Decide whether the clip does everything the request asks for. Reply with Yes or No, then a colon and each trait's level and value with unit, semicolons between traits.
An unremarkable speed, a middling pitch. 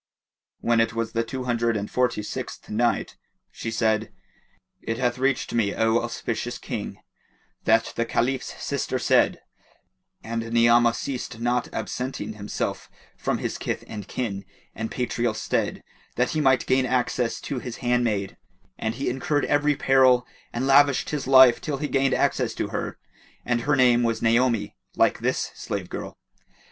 No: average, 155 wpm; low, 120 Hz